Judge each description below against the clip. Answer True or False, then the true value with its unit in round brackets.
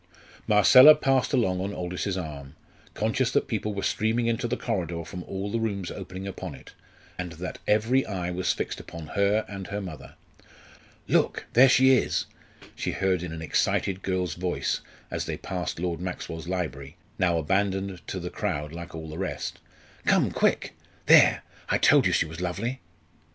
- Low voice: True (95 Hz)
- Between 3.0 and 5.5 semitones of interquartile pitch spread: True (3.4 semitones)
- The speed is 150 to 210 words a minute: True (170 wpm)